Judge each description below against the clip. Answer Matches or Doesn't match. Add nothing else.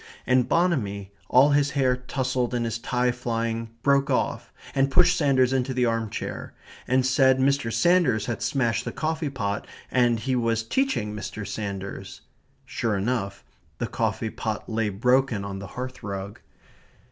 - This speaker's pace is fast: Doesn't match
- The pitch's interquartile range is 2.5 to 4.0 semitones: Matches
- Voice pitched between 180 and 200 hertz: Doesn't match